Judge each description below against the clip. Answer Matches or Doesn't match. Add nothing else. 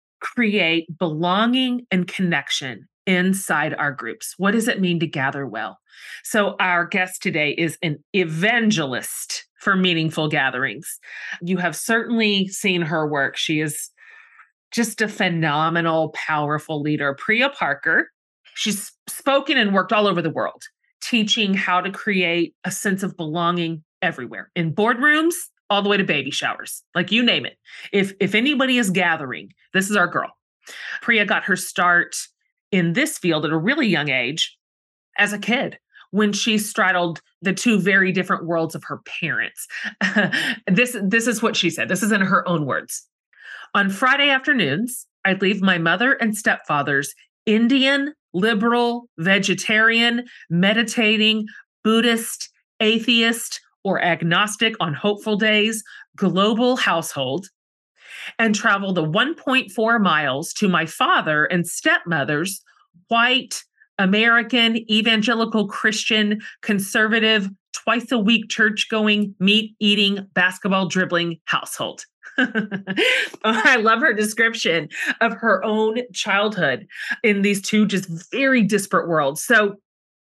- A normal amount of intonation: Matches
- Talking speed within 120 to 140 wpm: Matches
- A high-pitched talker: Matches